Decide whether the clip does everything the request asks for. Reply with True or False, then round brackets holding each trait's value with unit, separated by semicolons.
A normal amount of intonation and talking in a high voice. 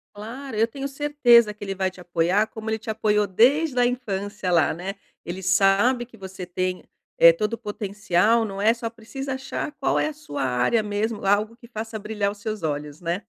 True (3.5 semitones; 210 Hz)